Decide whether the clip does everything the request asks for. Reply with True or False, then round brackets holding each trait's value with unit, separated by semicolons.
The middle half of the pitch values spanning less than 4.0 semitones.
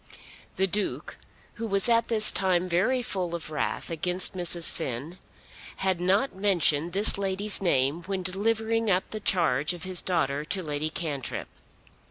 True (3.3 semitones)